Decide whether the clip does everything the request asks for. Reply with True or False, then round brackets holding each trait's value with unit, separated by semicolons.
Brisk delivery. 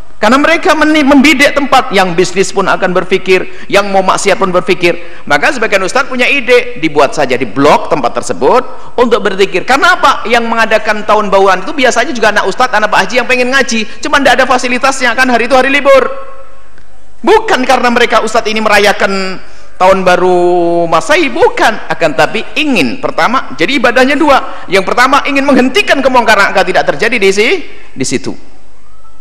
True (170 wpm)